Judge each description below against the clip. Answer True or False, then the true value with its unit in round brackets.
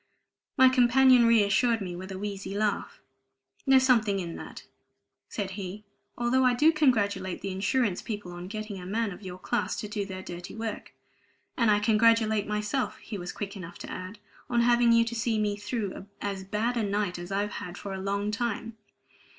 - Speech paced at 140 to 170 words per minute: False (190 wpm)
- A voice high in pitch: True (210 Hz)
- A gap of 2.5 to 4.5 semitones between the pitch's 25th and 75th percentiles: True (3.1 semitones)